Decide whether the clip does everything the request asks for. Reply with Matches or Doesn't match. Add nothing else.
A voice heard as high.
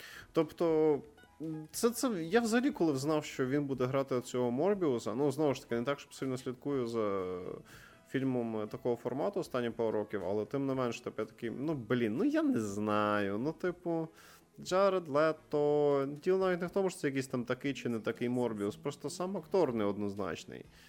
Doesn't match